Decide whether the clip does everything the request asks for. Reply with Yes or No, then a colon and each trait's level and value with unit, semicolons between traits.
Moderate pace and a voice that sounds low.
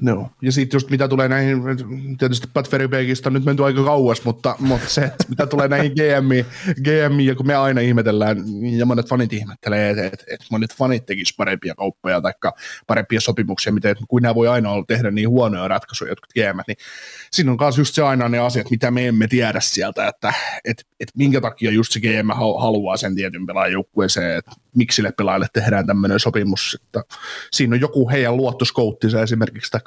No: fast, 195 wpm; low, 120 Hz